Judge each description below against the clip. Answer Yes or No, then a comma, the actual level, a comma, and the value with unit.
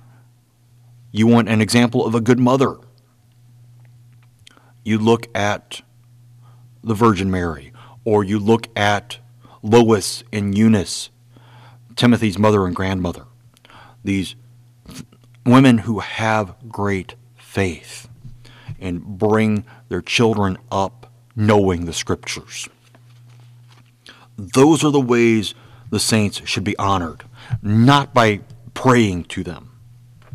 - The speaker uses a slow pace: Yes, slow, 105 wpm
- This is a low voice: Yes, low, 120 Hz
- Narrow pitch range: Yes, narrow, 2.3 semitones